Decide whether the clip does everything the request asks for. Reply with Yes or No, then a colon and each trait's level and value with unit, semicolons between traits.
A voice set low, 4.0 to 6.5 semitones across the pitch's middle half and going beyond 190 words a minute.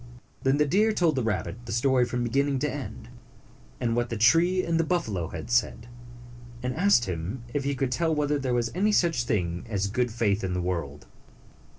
Yes: low, 125 Hz; wide, 5.5 semitones; fast, 205 wpm